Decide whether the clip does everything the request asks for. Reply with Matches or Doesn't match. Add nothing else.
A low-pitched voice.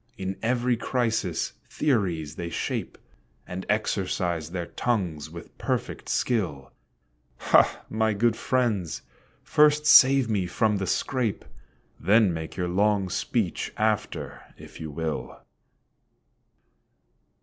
Matches